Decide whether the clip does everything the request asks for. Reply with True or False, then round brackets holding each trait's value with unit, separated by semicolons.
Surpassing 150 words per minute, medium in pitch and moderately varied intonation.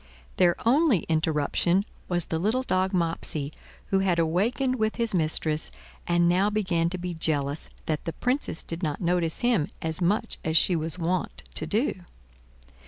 True (165 wpm; 175 Hz; 3.8 semitones)